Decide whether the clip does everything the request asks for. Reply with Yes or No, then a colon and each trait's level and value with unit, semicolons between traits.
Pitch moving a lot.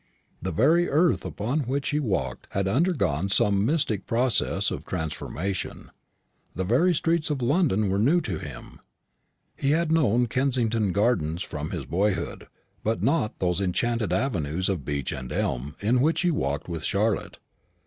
Yes: wide, 7.3 semitones